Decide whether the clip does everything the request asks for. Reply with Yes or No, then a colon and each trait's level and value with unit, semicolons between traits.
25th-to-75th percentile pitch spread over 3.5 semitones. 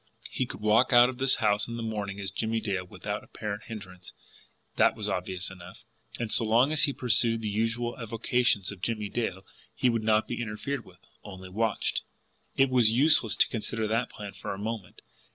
No: average, 2.7 semitones